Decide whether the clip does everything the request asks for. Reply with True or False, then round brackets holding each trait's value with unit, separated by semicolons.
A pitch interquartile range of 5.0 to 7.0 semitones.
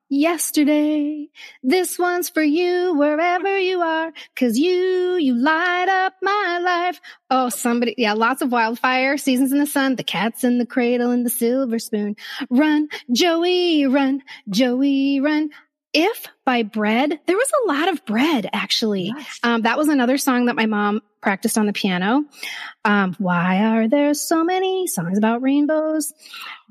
True (5.6 semitones)